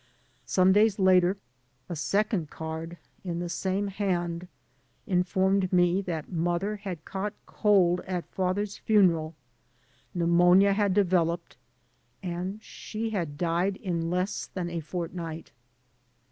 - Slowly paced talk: Yes, slow, 120 wpm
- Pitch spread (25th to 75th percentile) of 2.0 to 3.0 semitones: Yes, narrow, 2.4 semitones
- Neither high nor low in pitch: Yes, medium, 180 Hz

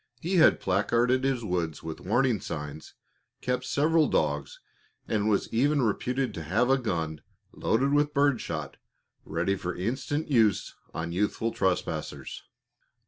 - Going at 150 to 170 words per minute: No, average, 140 wpm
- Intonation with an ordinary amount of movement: No, wide, 7.2 semitones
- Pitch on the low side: Yes, low, 115 Hz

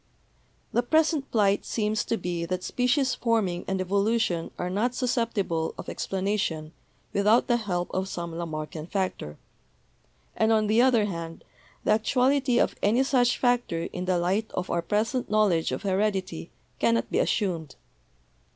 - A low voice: No, high, 205 Hz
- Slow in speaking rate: No, average, 150 wpm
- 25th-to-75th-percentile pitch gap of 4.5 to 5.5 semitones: Yes, average, 4.9 semitones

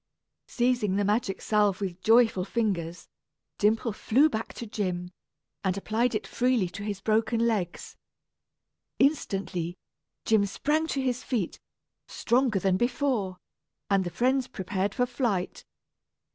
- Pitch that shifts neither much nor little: Yes, average, 4.2 semitones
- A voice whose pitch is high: Yes, high, 215 Hz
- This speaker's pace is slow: Yes, slow, 130 wpm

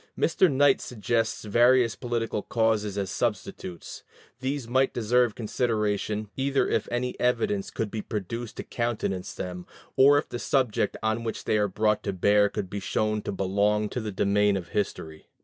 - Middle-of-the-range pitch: No, low, 110 Hz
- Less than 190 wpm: Yes, average, 165 wpm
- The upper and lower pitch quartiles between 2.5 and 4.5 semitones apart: Yes, average, 3.0 semitones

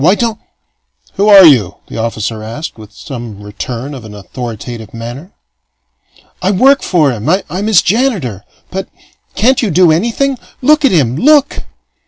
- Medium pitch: Yes, medium, 155 Hz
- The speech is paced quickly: No, average, 160 wpm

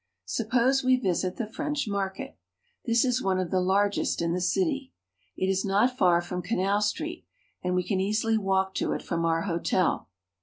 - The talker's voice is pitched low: No, high, 195 Hz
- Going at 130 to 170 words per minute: No, average, 185 wpm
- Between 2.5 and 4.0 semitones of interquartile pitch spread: No, average, 4.4 semitones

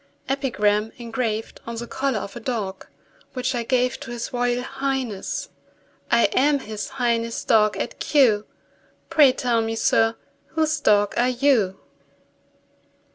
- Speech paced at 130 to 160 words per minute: Yes, slow, 135 wpm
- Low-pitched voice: No, high, 240 Hz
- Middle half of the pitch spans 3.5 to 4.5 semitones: No, average, 3.0 semitones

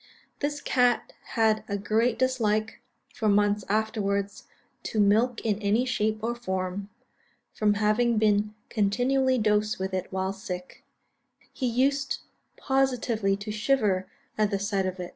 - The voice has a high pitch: Yes, high, 215 Hz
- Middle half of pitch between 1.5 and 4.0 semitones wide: Yes, average, 3.0 semitones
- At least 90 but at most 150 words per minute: Yes, average, 140 wpm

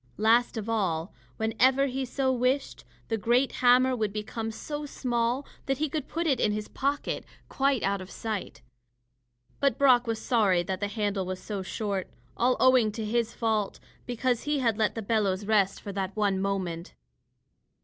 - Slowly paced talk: No, average, 175 wpm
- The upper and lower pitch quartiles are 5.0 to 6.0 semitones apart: No, average, 4.1 semitones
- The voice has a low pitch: No, high, 225 Hz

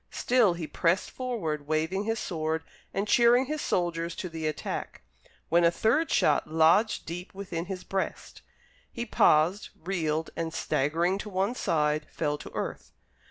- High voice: No, medium, 175 Hz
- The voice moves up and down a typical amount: Yes, average, 4.3 semitones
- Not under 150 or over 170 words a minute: Yes, average, 155 wpm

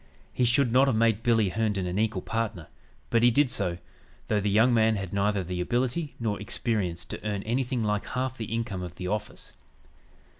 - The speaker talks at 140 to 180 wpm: No, average, 195 wpm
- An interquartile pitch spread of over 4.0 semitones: No, average, 3.2 semitones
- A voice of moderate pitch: No, low, 110 Hz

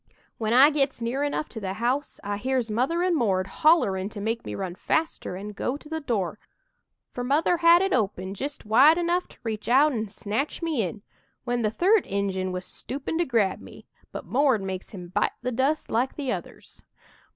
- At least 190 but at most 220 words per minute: Yes, average, 200 wpm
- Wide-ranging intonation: Yes, wide, 6.4 semitones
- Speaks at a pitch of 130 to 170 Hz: No, high, 245 Hz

